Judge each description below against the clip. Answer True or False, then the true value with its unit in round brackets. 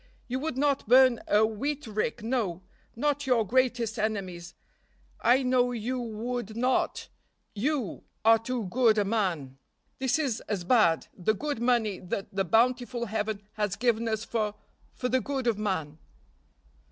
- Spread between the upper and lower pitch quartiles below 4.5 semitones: True (3.3 semitones)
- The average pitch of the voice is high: True (230 Hz)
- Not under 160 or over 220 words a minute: False (150 wpm)